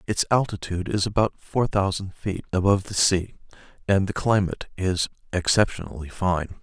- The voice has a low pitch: Yes, very low, 95 Hz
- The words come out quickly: No, average, 145 wpm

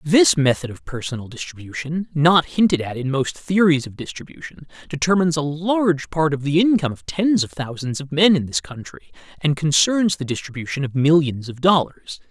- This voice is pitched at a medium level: Yes, medium, 155 Hz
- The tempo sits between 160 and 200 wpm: Yes, average, 180 wpm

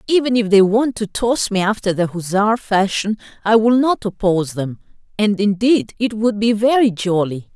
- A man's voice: No, female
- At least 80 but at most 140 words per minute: No, average, 185 wpm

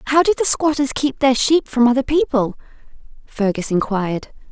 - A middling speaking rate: Yes, average, 160 wpm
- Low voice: No, very high, 260 Hz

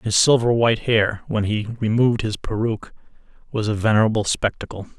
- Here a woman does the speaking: No, male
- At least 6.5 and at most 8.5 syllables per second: No, 5.8 syllables/s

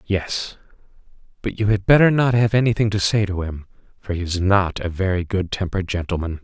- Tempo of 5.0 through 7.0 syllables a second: Yes, 5.6 syllables/s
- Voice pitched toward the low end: Yes, very low, 95 Hz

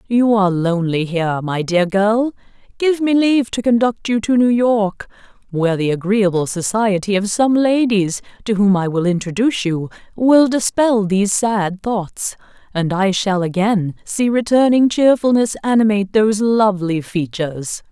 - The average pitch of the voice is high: Yes, high, 205 Hz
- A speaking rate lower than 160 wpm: Yes, average, 150 wpm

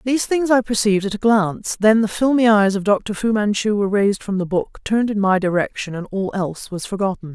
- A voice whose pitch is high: Yes, high, 205 Hz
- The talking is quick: Yes, fast, 235 wpm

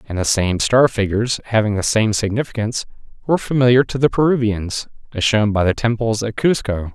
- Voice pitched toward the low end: Yes, low, 110 Hz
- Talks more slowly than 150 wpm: No, average, 180 wpm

